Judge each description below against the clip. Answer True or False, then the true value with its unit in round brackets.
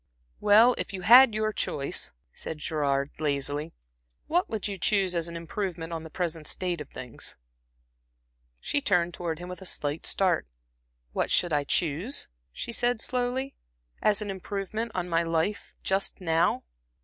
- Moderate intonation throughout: True (4.6 semitones)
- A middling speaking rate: True (160 wpm)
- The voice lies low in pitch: False (180 Hz)